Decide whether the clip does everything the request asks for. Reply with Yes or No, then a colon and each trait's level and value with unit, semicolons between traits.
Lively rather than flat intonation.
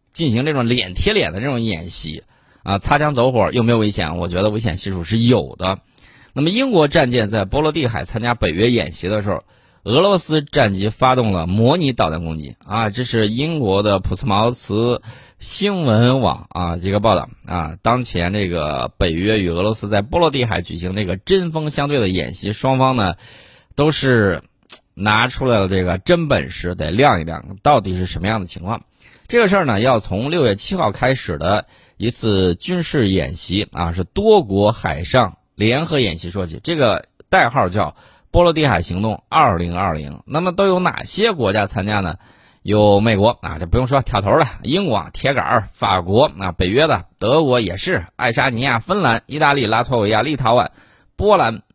Yes: wide, 5.8 semitones